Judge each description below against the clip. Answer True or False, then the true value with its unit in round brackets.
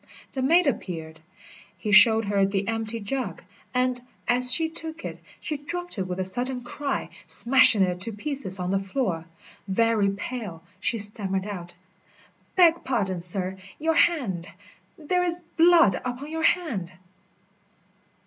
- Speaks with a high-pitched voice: True (230 Hz)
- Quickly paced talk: False (145 wpm)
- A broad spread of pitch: True (6.8 semitones)